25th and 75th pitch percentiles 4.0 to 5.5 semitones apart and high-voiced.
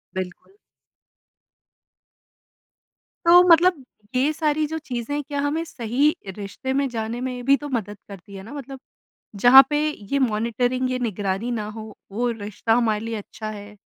Yes: average, 4.7 semitones; high, 245 Hz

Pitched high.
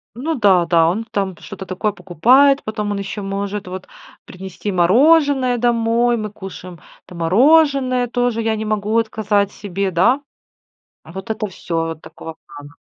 Yes: high, 210 Hz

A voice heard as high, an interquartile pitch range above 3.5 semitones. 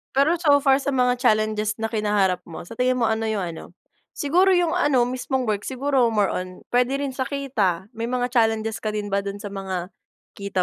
Yes: high, 225 Hz; average, 4.3 semitones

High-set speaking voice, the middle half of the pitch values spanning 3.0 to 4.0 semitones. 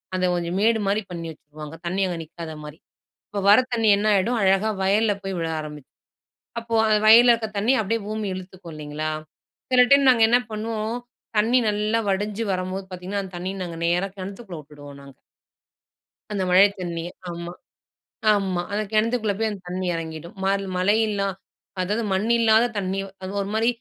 Yes: high, 195 Hz; average, 3.7 semitones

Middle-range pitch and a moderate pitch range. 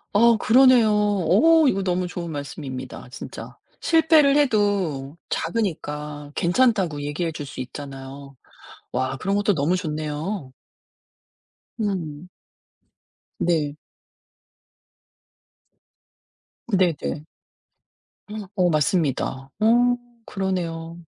No: medium, 175 Hz; wide, 5.9 semitones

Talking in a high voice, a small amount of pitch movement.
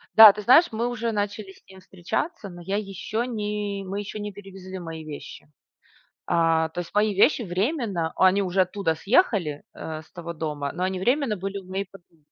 No: high, 195 Hz; average, 3.2 semitones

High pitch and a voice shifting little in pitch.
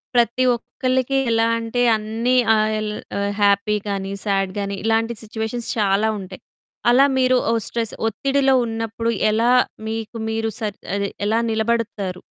Yes: high, 225 Hz; narrow, 2.0 semitones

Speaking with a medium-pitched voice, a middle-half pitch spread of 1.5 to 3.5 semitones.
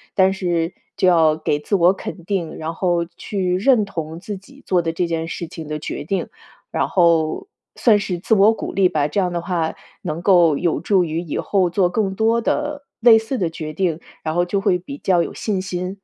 Yes: medium, 180 Hz; average, 3.1 semitones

